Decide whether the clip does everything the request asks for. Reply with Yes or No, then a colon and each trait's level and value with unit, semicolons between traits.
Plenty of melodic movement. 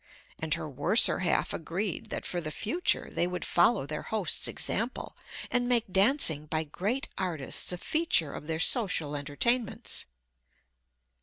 Yes: wide, 6.6 semitones